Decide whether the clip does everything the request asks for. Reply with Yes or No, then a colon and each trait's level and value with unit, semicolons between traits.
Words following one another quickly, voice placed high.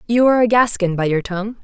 Yes: fast, 255 wpm; high, 210 Hz